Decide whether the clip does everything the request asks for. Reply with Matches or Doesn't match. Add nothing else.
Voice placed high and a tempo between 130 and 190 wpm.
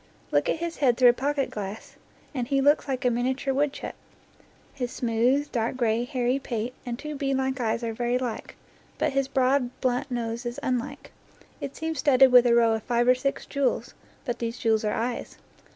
Doesn't match